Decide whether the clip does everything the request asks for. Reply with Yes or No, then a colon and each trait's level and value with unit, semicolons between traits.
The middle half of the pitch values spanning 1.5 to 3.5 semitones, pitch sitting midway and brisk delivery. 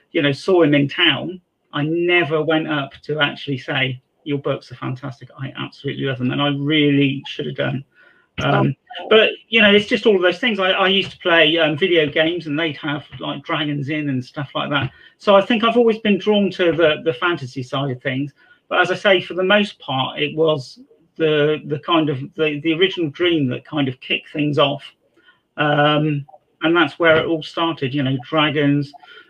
No: average, 3.9 semitones; medium, 155 Hz; fast, 210 wpm